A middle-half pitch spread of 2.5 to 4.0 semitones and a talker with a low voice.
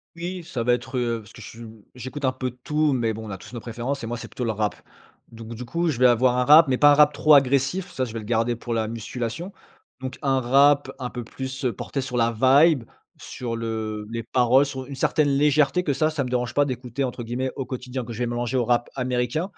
Yes: average, 2.9 semitones; low, 125 Hz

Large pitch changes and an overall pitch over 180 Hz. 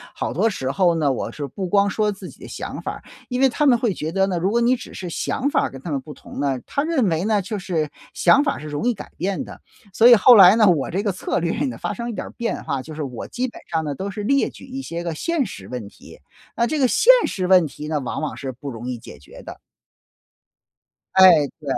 Yes: wide, 7.5 semitones; high, 190 Hz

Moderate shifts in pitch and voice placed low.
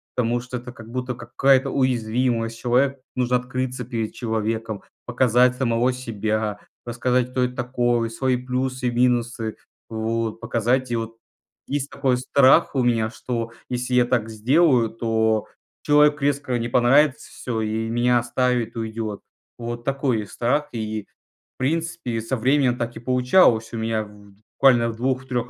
No: narrow, 2.1 semitones; low, 120 Hz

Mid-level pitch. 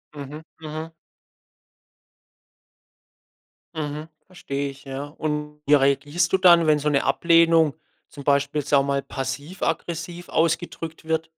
Yes: medium, 150 Hz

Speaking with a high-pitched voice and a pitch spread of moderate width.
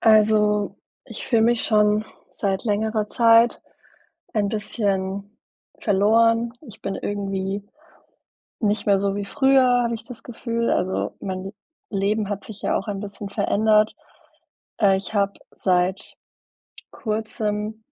No: high, 210 Hz; narrow, 2.0 semitones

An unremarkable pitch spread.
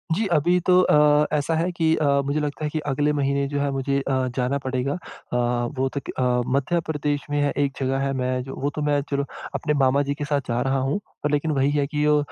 No: narrow, 1.7 semitones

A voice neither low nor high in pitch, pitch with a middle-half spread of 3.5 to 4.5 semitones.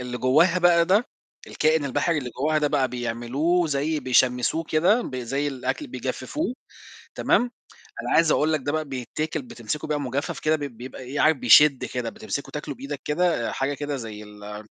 Yes: medium, 145 Hz; average, 3.9 semitones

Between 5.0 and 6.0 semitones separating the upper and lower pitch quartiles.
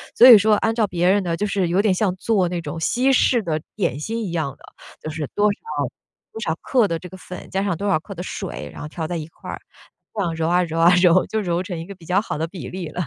No: average, 3.6 semitones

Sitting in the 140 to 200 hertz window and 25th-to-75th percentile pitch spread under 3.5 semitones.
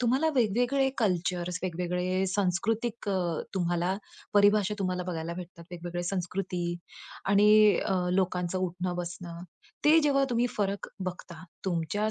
Yes: medium, 185 Hz; average, 2.8 semitones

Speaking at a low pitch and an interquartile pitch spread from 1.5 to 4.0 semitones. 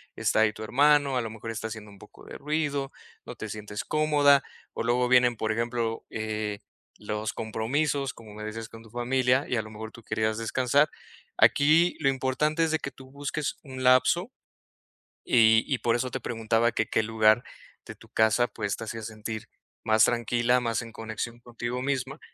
Yes: low, 120 Hz; average, 3.3 semitones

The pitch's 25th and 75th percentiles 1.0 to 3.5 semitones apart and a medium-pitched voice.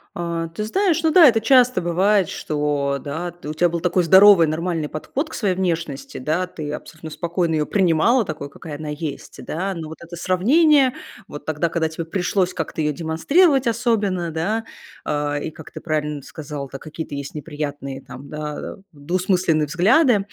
No: average, 4.4 semitones; medium, 165 Hz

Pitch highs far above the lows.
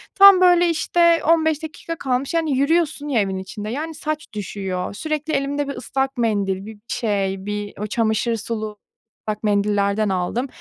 Yes: wide, 7.1 semitones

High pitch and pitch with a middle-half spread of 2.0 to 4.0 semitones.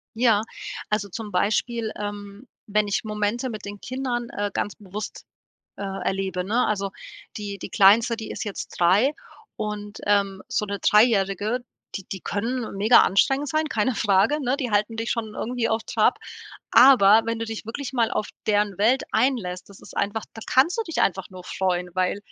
Yes: high, 210 Hz; average, 2.8 semitones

